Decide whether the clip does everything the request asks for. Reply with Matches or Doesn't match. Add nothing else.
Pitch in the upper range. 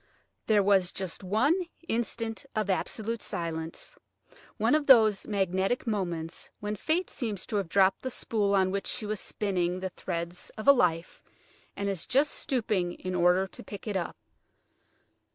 Matches